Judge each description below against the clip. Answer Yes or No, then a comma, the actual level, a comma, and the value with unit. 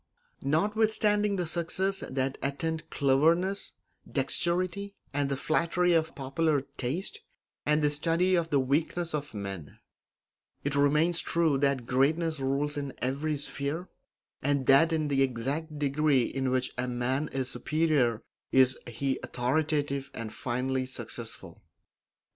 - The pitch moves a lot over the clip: No, average, 3.6 semitones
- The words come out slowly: Yes, slow, 130 wpm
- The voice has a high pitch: No, medium, 145 Hz